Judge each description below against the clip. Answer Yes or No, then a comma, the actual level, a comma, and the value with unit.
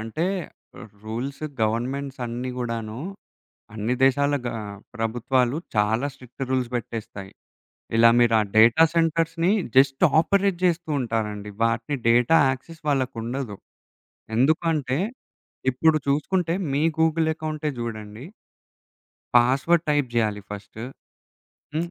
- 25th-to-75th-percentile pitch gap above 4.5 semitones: Yes, average, 5.2 semitones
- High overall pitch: No, low, 130 Hz